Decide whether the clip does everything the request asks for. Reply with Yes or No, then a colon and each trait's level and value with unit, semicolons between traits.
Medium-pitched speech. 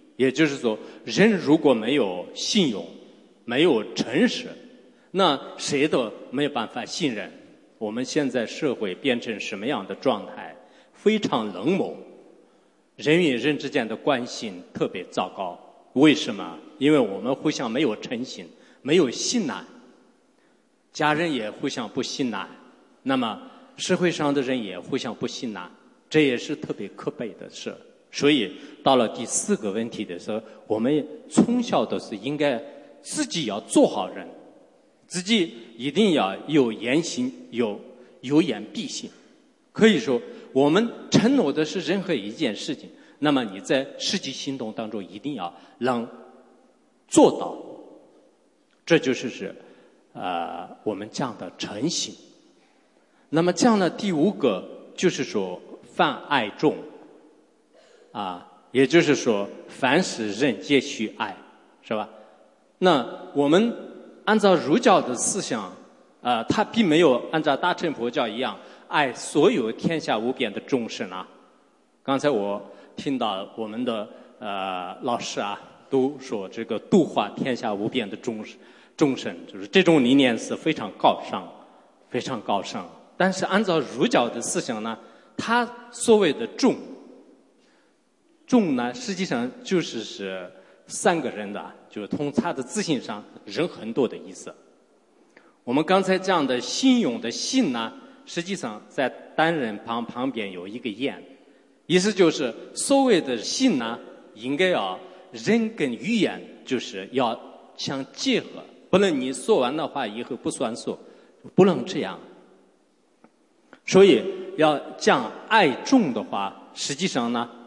Yes: medium, 175 Hz